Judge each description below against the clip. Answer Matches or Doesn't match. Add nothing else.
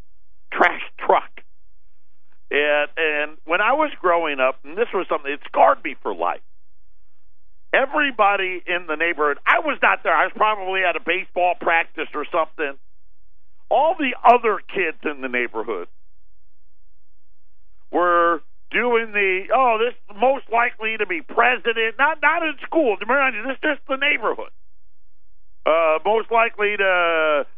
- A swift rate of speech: Doesn't match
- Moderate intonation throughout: Doesn't match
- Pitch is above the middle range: Doesn't match